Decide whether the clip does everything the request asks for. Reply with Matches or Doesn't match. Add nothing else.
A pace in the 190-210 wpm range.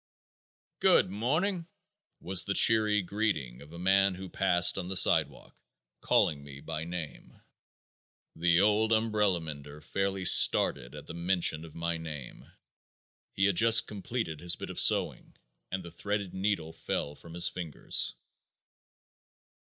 Doesn't match